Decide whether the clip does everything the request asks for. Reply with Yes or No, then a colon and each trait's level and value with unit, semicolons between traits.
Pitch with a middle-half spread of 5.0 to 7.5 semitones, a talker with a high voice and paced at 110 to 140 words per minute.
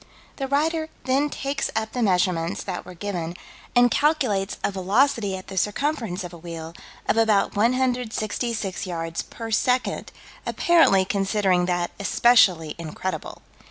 Yes: wide, 5.6 semitones; high, 205 Hz; slow, 135 wpm